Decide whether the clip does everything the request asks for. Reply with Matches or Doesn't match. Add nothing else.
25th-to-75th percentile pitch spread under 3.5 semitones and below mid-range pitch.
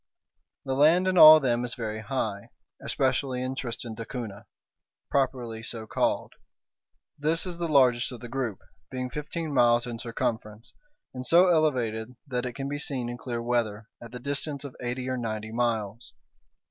Matches